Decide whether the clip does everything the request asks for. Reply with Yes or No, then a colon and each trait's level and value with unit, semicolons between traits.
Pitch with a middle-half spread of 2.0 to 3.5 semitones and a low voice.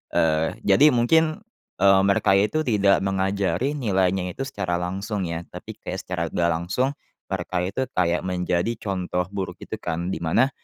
Yes: average, 3.2 semitones; very low, 95 Hz